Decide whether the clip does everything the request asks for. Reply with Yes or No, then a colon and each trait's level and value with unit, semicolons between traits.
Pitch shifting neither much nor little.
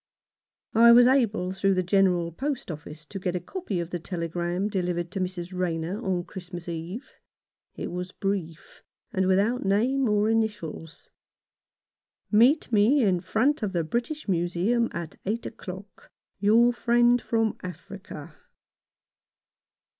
Yes: average, 4.4 semitones